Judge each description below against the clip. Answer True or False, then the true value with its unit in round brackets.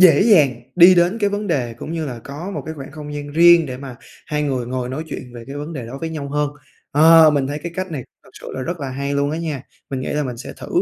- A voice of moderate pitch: True (145 Hz)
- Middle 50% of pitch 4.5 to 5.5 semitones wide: False (3.6 semitones)